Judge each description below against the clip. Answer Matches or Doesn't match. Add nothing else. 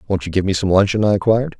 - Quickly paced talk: Matches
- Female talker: Doesn't match